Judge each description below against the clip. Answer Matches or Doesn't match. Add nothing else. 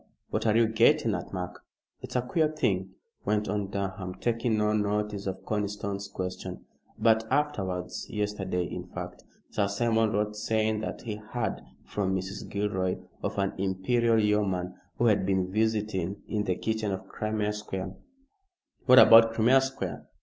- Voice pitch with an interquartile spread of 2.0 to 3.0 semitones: Matches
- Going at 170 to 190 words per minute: Doesn't match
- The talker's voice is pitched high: Doesn't match